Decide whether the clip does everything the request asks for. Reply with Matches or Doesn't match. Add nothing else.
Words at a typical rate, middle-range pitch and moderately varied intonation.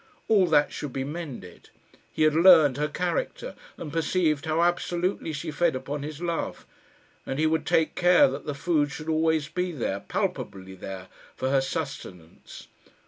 Matches